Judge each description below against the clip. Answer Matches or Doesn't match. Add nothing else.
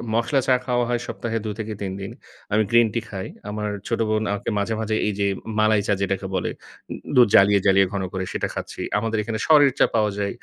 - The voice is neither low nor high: Doesn't match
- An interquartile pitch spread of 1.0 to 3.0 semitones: Matches